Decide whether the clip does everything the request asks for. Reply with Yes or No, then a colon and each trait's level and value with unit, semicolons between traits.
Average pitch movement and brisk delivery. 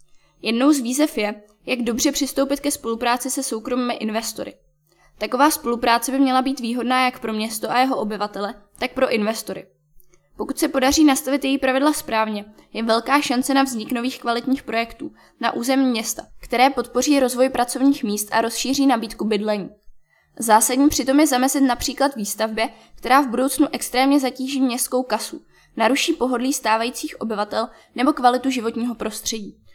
No: average, 3.3 semitones; average, 150 wpm